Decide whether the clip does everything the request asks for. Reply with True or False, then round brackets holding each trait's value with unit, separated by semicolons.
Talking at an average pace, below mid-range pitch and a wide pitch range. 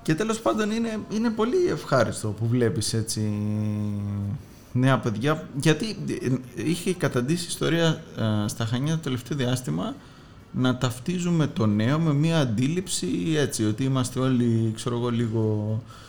True (135 wpm; 125 Hz; 6.1 semitones)